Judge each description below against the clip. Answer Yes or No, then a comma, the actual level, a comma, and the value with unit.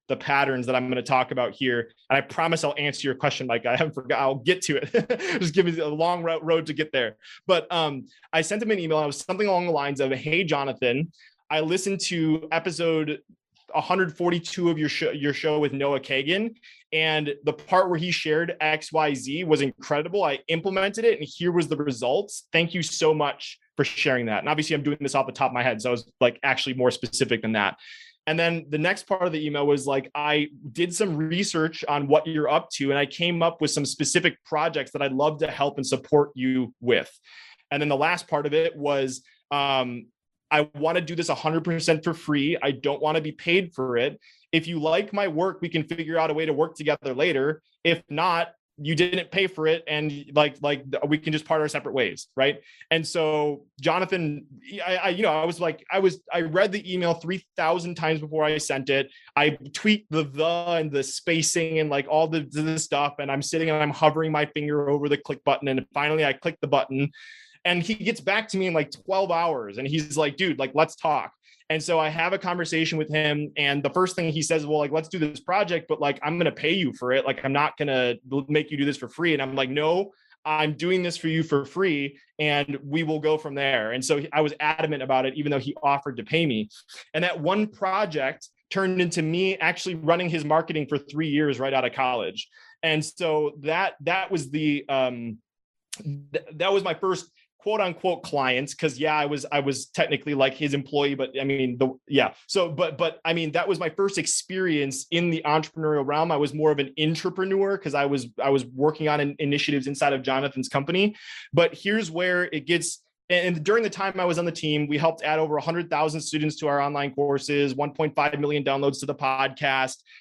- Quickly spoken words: Yes, fast, 225 wpm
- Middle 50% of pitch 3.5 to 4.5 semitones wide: No, average, 3.0 semitones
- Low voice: No, medium, 155 Hz